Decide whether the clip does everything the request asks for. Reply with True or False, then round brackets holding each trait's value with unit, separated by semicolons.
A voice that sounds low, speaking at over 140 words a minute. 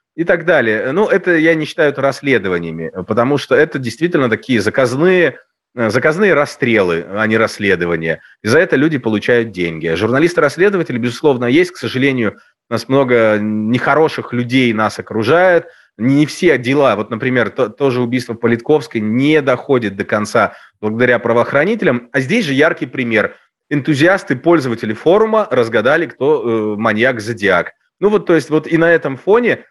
True (125 Hz; 150 wpm)